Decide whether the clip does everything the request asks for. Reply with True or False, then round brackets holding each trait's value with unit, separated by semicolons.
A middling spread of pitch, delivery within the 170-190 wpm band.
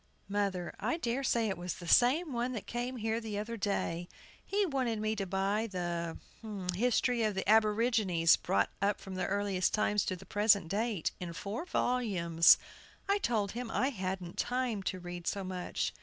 True (4.2 semitones; 175 wpm)